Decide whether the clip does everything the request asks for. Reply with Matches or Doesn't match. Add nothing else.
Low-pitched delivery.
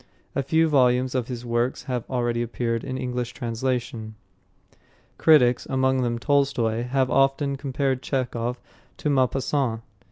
Matches